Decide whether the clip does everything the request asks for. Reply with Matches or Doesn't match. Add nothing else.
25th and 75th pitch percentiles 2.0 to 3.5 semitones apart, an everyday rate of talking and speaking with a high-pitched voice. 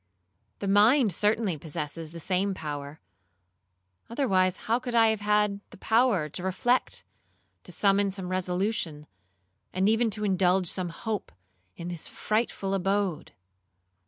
Doesn't match